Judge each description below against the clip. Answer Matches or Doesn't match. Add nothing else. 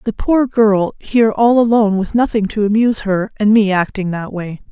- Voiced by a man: Doesn't match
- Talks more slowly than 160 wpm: Doesn't match